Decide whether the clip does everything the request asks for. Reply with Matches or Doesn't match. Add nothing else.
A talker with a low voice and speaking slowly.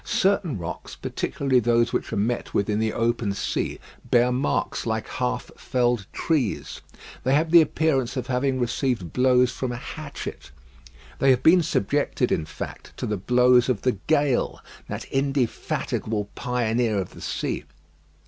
Doesn't match